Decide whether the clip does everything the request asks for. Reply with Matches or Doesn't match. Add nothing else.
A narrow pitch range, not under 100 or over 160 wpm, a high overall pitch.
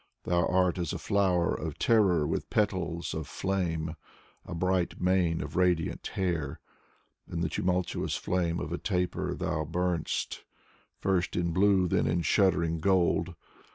Doesn't match